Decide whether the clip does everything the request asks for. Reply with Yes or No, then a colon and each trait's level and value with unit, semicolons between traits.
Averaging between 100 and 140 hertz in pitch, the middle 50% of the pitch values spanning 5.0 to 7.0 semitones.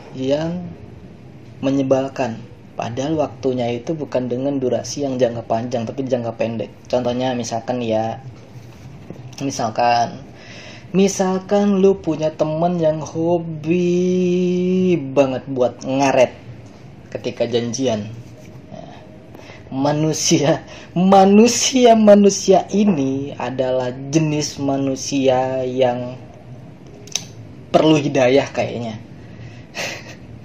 No: low, 135 Hz; average, 4.5 semitones